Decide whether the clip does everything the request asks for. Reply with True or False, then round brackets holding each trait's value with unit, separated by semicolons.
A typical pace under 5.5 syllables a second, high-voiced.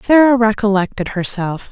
True (5.0 syllables/s; 215 Hz)